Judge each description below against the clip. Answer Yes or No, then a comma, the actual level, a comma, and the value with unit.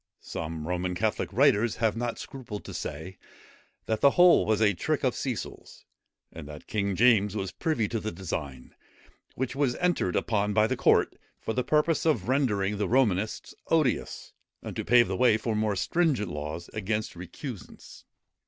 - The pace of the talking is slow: No, average, 170 wpm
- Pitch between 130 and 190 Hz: No, low, 110 Hz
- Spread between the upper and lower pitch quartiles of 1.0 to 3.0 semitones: No, average, 4.9 semitones